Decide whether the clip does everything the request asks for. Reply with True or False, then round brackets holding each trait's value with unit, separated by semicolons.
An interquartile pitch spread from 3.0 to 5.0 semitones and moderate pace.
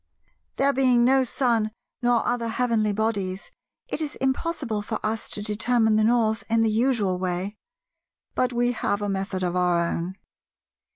True (3.3 semitones; 160 wpm)